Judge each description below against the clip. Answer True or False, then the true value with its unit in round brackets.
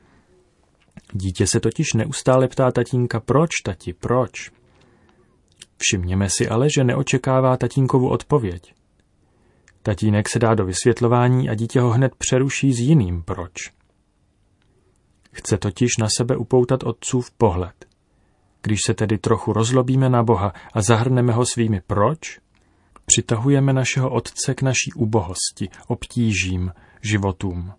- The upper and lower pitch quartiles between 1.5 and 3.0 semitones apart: False (4.1 semitones)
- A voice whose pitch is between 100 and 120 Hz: True (115 Hz)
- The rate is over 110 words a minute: True (120 wpm)